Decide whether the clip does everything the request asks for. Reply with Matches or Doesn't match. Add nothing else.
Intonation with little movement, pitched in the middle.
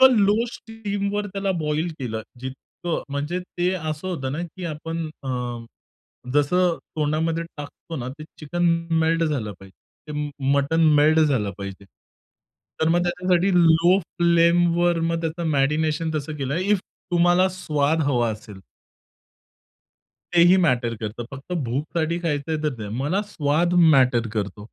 Doesn't match